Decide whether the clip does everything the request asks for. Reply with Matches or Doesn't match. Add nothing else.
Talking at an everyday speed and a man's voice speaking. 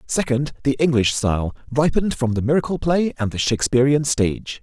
Matches